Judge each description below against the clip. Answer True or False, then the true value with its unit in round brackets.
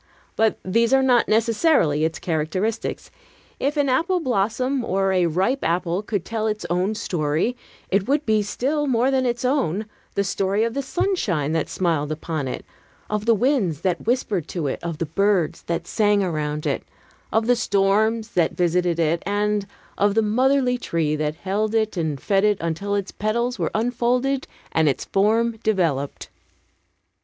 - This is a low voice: False (205 Hz)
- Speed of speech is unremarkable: True (170 wpm)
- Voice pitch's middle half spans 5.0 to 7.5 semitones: True (5.6 semitones)